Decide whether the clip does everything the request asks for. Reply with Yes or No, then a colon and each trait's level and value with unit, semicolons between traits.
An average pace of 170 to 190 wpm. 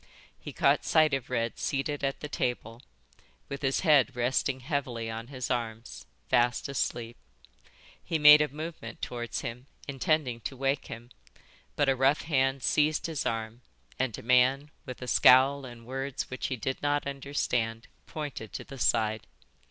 No: average, 160 wpm